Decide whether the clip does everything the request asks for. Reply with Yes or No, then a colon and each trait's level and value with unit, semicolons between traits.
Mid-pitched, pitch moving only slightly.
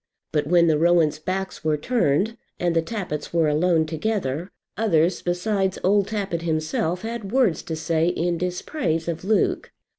No: medium, 175 Hz; average, 3.5 semitones